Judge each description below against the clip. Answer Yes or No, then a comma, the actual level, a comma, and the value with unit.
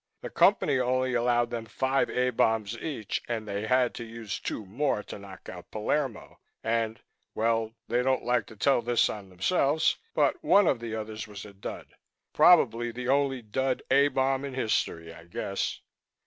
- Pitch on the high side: No, low, 120 Hz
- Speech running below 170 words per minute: No, average, 175 wpm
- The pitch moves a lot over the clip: No, average, 3.4 semitones